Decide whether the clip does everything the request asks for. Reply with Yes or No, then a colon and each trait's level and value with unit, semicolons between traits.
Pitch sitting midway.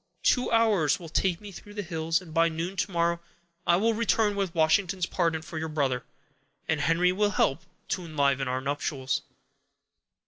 Yes: medium, 170 Hz